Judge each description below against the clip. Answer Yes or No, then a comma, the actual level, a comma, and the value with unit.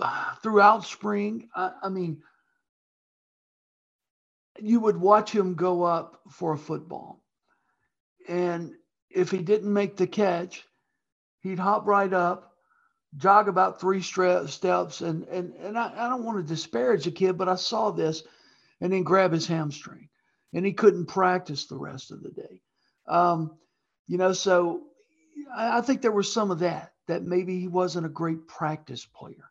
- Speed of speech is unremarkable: Yes, average, 160 wpm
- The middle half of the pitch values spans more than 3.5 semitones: No, average, 3.2 semitones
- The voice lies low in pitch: No, medium, 185 Hz